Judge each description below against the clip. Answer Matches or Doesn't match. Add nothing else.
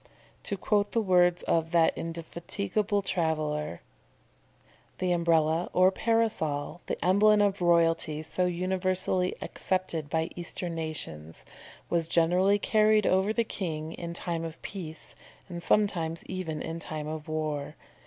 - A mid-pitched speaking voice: Matches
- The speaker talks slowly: Matches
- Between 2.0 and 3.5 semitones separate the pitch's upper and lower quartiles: Matches